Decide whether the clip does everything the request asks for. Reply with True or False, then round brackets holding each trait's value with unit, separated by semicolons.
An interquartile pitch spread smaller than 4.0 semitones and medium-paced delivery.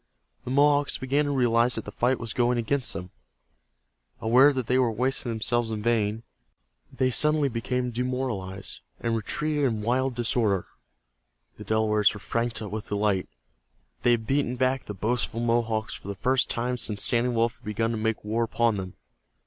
True (2.6 semitones; 175 wpm)